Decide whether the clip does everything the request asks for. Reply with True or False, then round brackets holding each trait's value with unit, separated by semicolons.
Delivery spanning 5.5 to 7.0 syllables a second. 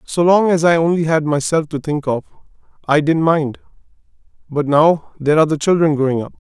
True (5.7 syllables/s)